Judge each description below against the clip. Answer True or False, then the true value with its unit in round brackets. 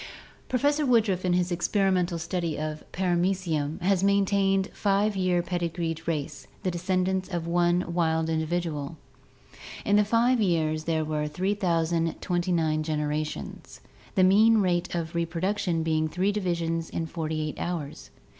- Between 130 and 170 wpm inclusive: True (135 wpm)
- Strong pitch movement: False (2.8 semitones)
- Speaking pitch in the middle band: True (175 Hz)